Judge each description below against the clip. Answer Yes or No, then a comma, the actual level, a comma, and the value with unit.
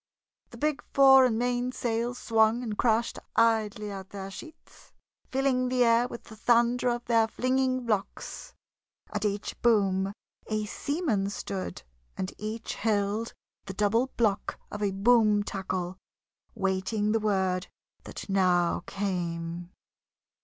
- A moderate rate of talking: No, slow, 130 wpm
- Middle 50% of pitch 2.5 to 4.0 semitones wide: Yes, average, 3.6 semitones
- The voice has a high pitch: Yes, high, 215 Hz